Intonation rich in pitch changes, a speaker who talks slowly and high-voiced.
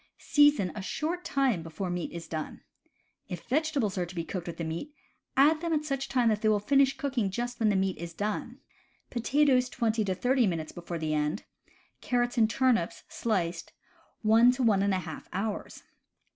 No: wide, 6.9 semitones; average, 190 wpm; high, 215 Hz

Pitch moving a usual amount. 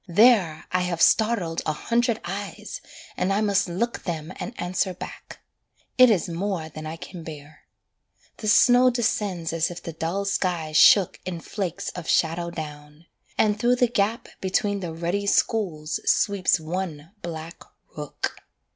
Yes: average, 4.0 semitones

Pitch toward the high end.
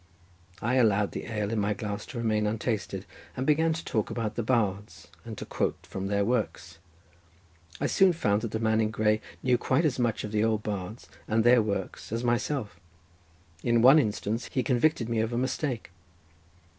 No: low, 110 Hz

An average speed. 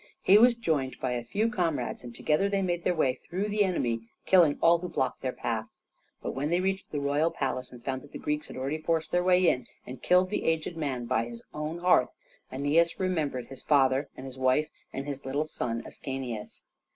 No: fast, 215 wpm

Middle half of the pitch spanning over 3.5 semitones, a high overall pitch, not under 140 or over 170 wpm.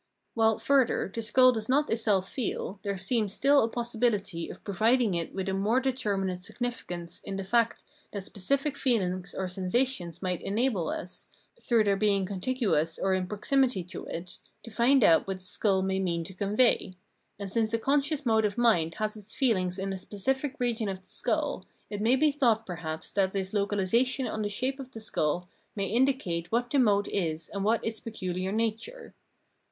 No: average, 4.3 semitones; high, 210 Hz; average, 190 wpm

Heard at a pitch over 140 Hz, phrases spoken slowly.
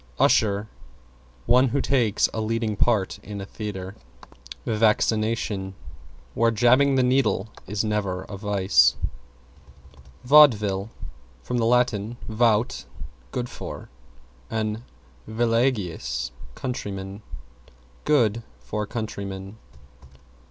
No: low, 110 Hz; slow, 90 wpm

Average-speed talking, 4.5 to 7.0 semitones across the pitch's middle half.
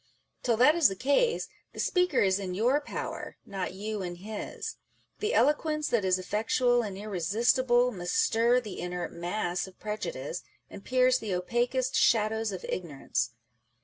Yes: average, 155 wpm; average, 5.3 semitones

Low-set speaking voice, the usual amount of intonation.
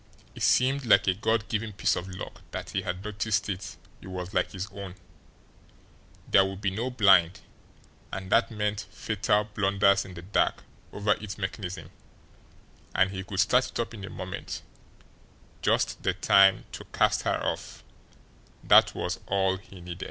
No: low, 100 Hz; narrow, 2.0 semitones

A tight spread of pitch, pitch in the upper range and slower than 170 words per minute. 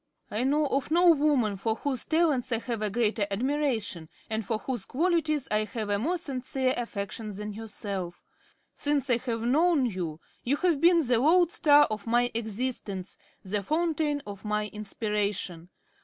No: wide, 5.6 semitones; high, 240 Hz; average, 160 wpm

